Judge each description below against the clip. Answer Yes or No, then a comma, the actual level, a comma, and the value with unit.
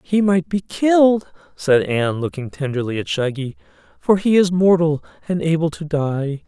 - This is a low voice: No, medium, 155 Hz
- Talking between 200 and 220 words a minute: No, average, 165 wpm